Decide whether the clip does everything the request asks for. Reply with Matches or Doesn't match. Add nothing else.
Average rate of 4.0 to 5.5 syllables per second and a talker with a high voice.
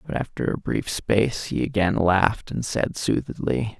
Doesn't match